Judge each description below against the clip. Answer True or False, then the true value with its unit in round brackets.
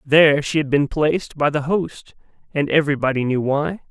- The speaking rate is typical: True (185 wpm)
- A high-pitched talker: False (150 Hz)